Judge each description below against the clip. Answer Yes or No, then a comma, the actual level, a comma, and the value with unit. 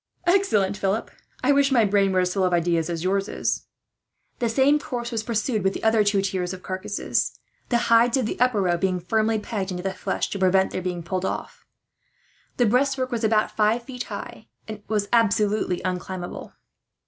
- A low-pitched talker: No, high, 210 Hz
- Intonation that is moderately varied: Yes, average, 3.9 semitones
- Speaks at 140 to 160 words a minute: No, average, 195 wpm